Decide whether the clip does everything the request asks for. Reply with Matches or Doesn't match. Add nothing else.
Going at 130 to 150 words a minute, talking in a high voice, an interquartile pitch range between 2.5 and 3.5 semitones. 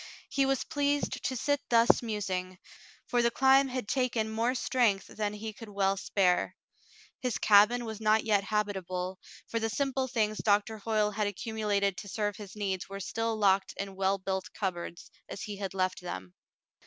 Doesn't match